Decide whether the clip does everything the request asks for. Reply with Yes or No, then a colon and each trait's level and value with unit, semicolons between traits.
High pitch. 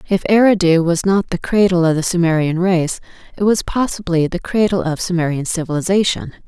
No: medium, 180 Hz